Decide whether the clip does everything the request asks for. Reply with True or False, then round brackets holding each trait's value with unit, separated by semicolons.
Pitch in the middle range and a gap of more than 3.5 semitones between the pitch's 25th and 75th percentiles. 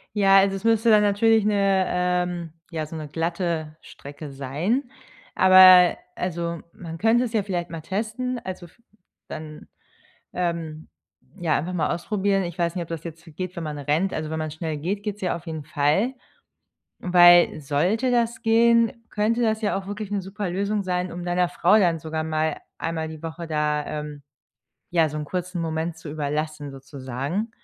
True (175 Hz; 4.1 semitones)